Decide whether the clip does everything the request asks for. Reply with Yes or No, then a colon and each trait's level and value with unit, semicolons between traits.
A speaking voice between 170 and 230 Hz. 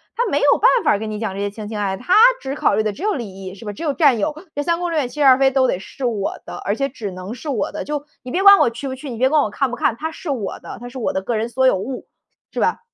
No: very high, 250 Hz